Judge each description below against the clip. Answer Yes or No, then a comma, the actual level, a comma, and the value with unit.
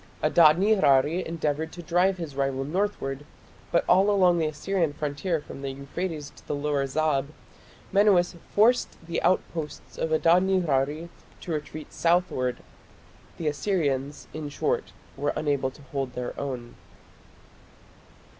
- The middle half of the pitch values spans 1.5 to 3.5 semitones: No, average, 4.1 semitones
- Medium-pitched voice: Yes, medium, 155 Hz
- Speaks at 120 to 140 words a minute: Yes, slow, 135 wpm